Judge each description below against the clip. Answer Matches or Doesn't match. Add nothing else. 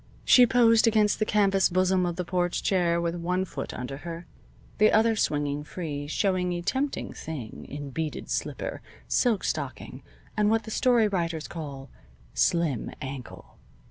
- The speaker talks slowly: Doesn't match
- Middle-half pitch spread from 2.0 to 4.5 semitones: Doesn't match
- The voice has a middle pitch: Matches